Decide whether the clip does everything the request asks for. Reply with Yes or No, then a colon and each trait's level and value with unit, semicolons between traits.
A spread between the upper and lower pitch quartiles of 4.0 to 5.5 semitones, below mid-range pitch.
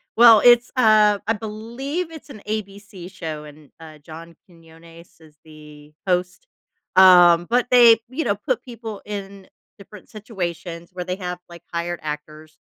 No: average, 4.9 semitones; medium, 185 Hz